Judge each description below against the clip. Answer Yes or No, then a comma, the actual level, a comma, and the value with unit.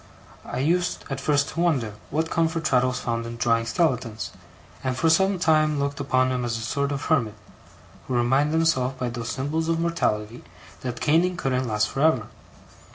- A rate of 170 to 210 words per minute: Yes, average, 180 wpm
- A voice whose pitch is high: No, low, 135 Hz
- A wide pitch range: No, average, 4.8 semitones